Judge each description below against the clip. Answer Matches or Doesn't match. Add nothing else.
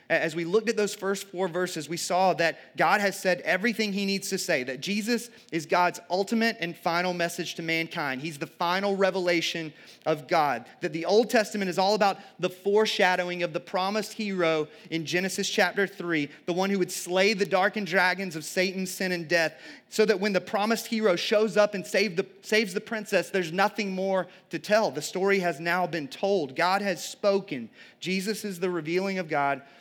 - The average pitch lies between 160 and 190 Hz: Matches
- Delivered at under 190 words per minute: Doesn't match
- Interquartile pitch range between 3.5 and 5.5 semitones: Doesn't match